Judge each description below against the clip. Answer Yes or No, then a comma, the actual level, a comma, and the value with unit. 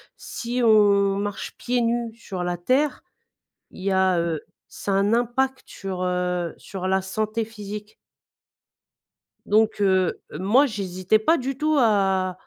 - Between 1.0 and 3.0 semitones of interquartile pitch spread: No, average, 3.7 semitones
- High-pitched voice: Yes, high, 205 Hz